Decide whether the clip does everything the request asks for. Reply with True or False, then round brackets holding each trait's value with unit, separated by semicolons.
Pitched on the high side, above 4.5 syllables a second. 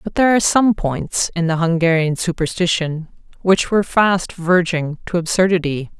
False (175 Hz; 5.0 syllables/s)